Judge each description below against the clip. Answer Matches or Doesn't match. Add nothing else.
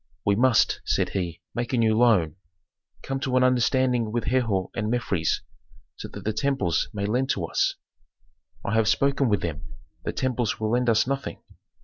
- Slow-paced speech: Doesn't match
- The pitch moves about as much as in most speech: Matches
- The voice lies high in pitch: Doesn't match